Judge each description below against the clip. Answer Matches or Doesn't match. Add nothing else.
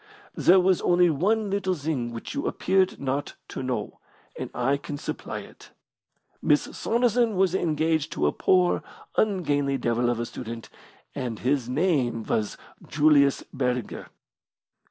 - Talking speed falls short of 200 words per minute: Matches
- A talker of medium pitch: Matches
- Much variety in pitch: Matches